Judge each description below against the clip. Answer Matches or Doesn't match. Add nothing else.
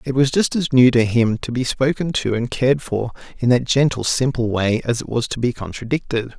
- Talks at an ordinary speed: Doesn't match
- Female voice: Doesn't match